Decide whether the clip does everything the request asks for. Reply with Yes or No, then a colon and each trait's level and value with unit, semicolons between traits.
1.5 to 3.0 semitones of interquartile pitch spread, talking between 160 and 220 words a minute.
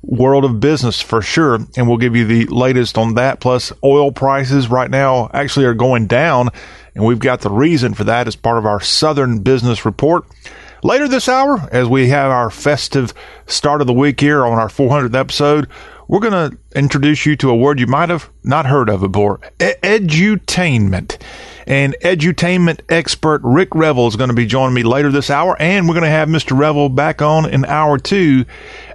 No: average, 3.7 semitones; average, 200 wpm